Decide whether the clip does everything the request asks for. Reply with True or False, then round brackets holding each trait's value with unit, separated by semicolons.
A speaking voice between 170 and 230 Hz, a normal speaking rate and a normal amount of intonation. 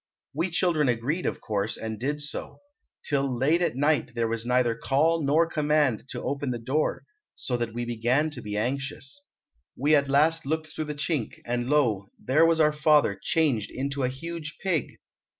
False (140 Hz; 185 wpm; 4.3 semitones)